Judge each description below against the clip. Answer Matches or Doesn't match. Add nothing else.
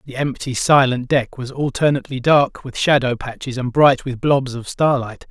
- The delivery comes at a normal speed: Matches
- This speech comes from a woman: Doesn't match